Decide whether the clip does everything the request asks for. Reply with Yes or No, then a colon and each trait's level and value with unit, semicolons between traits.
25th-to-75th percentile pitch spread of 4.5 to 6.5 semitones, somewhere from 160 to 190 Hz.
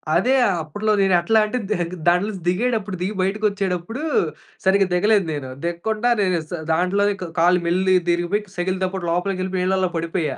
No: average, 2.7 semitones; medium, 185 Hz